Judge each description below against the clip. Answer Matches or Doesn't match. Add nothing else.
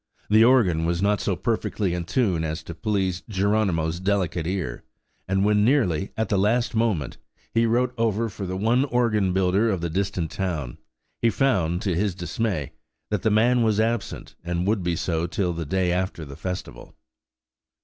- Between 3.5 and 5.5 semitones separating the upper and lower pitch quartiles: Matches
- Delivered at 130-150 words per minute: Doesn't match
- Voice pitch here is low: Matches